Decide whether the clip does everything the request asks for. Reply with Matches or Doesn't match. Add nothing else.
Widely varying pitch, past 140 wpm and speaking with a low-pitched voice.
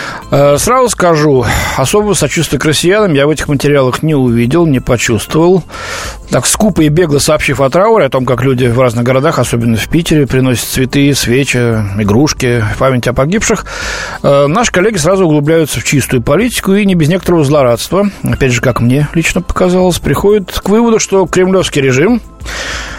Doesn't match